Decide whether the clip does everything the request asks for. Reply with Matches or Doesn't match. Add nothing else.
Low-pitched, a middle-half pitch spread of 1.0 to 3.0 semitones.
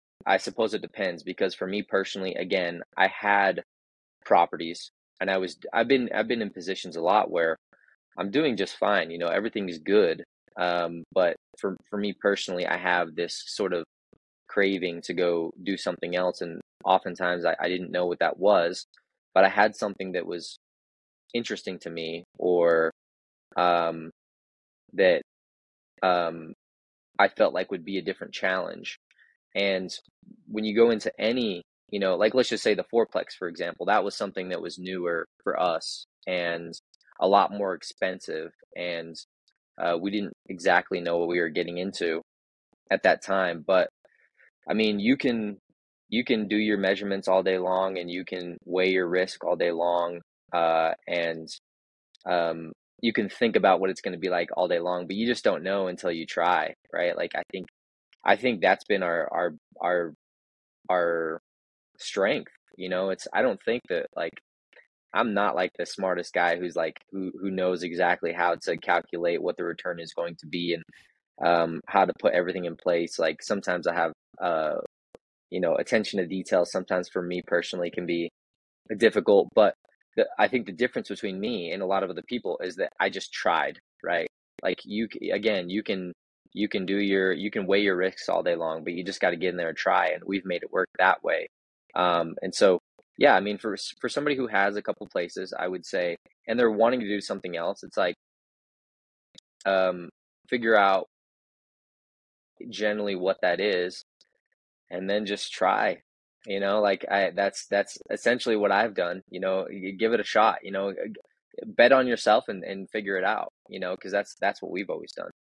Matches